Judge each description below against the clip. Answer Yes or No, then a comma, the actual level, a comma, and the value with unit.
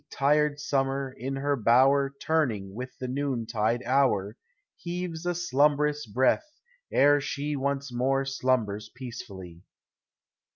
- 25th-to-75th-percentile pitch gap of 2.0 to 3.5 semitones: Yes, average, 3.1 semitones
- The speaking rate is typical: No, slow, 115 wpm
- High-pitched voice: No, low, 135 Hz